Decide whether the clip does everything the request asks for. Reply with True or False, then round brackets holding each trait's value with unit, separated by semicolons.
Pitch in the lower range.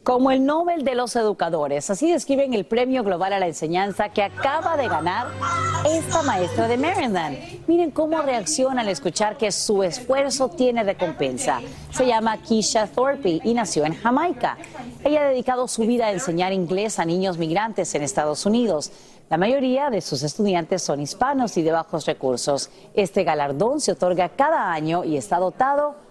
False (210 Hz)